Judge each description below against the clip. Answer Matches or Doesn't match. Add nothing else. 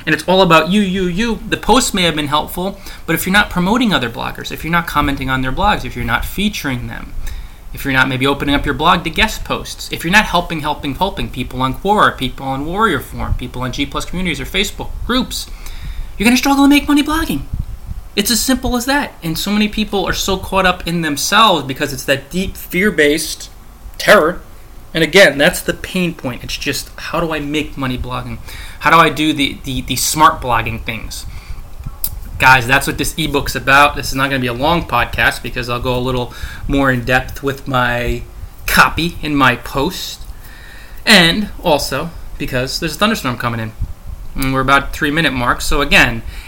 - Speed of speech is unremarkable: Doesn't match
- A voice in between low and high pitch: Matches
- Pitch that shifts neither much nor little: Doesn't match